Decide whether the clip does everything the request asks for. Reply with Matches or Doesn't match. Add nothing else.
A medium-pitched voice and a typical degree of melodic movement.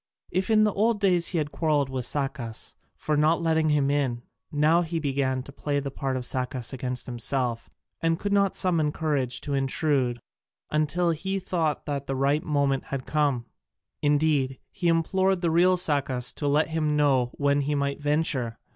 Matches